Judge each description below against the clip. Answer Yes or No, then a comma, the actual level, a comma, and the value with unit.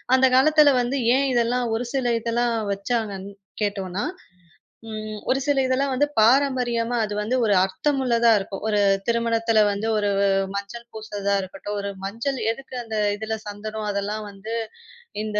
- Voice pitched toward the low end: No, high, 225 Hz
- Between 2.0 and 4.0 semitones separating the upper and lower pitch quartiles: Yes, average, 3.3 semitones